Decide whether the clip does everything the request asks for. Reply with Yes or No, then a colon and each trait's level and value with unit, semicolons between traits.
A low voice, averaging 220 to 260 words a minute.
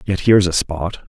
No: very low, 95 Hz; fast, 210 wpm